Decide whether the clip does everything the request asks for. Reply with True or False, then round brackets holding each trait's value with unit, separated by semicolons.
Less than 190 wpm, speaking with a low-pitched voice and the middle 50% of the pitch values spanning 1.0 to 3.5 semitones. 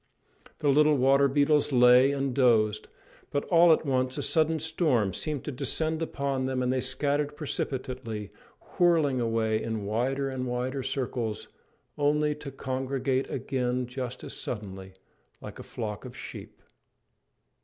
True (145 wpm; 130 Hz; 2.7 semitones)